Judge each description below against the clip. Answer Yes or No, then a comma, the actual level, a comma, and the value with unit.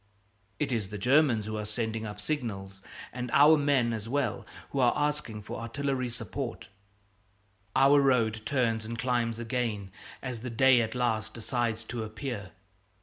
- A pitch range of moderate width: Yes, average, 3.0 semitones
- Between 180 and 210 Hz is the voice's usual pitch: No, low, 115 Hz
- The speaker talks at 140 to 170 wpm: Yes, average, 155 wpm